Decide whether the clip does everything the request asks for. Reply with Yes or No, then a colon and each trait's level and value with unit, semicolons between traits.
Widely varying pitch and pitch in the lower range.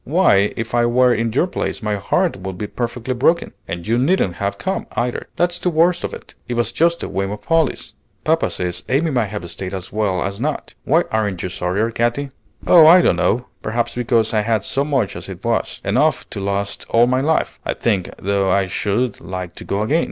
Yes: wide, 5.7 semitones; low, 115 Hz